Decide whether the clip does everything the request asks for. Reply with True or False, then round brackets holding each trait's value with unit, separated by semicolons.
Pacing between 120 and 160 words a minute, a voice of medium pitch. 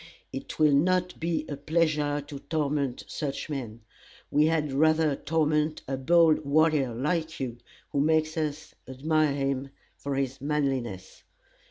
True (140 wpm; 150 Hz)